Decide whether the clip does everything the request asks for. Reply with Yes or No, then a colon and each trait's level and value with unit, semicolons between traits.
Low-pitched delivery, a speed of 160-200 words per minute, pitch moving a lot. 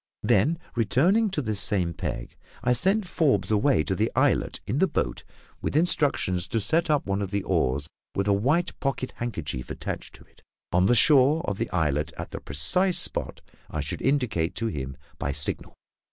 Yes: low, 110 Hz; average, 185 wpm; wide, 9.0 semitones